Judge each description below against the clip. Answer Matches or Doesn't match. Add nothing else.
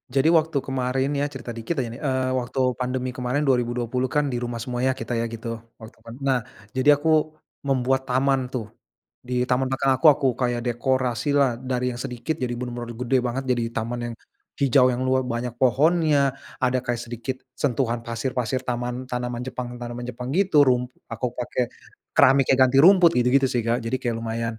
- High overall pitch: Doesn't match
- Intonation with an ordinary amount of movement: Doesn't match